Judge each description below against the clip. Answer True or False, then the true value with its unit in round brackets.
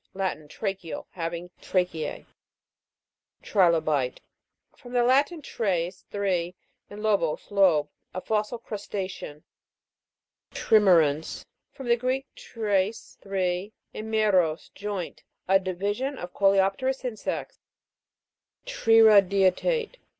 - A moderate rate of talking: False (90 wpm)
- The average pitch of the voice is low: False (195 Hz)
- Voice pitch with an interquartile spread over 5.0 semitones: False (3.8 semitones)